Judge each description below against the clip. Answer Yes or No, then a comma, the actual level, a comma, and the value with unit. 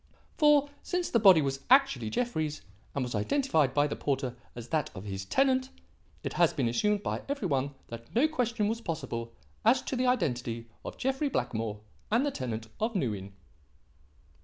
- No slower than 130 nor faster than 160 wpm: No, average, 180 wpm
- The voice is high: No, medium, 155 Hz